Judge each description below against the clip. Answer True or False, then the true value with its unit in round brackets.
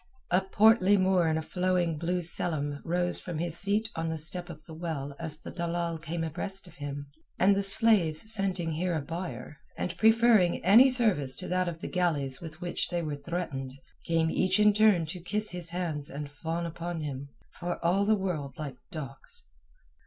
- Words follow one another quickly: False (190 wpm)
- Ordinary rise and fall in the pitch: True (3.2 semitones)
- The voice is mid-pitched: True (170 Hz)